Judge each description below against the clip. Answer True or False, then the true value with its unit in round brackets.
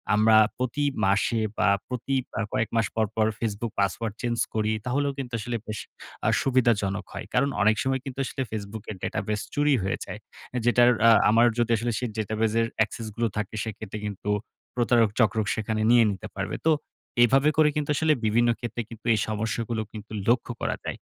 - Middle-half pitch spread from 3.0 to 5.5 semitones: False (2.4 semitones)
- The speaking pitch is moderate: False (115 Hz)